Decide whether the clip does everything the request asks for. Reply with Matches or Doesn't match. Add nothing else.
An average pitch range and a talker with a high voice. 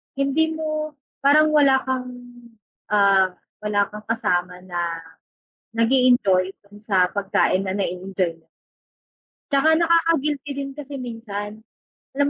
Doesn't match